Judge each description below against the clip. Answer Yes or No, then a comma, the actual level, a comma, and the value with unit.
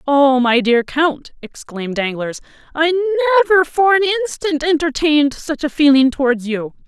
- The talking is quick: No, average, 150 wpm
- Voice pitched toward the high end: Yes, very high, 300 Hz